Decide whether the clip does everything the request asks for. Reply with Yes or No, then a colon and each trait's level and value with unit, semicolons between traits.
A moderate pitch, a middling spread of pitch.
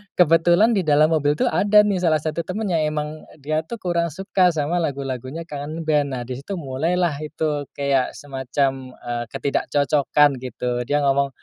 Yes: medium, 150 Hz; average, 3.4 semitones